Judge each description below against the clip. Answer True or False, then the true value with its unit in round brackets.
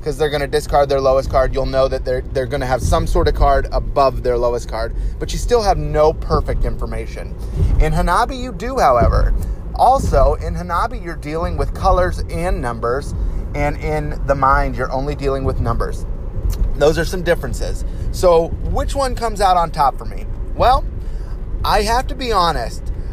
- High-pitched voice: False (135 Hz)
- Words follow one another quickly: False (180 wpm)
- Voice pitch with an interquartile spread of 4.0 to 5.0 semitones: True (4.7 semitones)